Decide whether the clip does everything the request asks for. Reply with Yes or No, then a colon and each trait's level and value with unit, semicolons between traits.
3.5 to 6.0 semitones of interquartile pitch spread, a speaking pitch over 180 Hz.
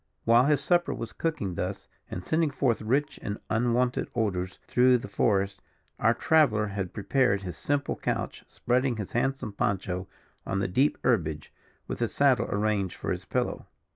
No: average, 4.7 semitones; low, 110 Hz